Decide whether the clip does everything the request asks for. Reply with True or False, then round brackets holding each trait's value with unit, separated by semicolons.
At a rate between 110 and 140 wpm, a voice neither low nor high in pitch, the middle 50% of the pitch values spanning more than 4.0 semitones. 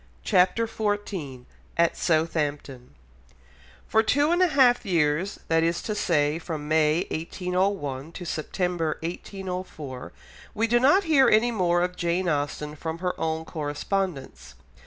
True (135 wpm; 175 Hz; 5.0 semitones)